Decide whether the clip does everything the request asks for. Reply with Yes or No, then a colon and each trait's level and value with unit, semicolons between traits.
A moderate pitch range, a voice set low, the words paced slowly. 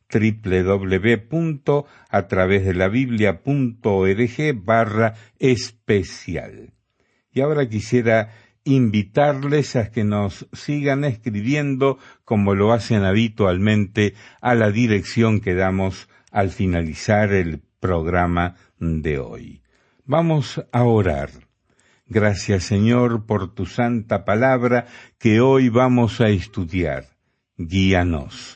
Yes: average, 4.3 semitones; low, 110 Hz; slow, 90 wpm